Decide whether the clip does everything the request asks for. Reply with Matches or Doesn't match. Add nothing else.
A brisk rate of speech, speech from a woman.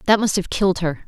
Matches